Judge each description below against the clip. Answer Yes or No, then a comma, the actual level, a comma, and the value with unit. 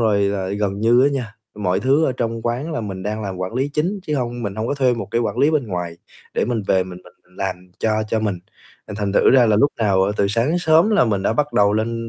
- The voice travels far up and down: No, average, 4.5 semitones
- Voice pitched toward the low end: Yes, low, 110 Hz